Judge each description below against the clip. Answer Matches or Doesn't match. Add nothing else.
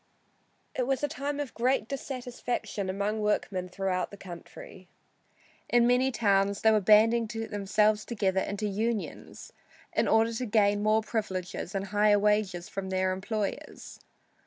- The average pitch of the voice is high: Matches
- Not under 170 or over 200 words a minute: Doesn't match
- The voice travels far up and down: Doesn't match